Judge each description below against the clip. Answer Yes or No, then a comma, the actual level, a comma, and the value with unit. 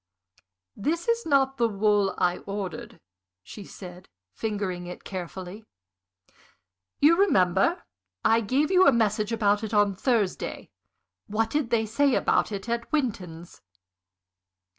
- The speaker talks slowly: Yes, slow, 125 wpm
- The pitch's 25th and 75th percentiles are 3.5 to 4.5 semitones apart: No, average, 5.1 semitones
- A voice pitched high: Yes, high, 215 Hz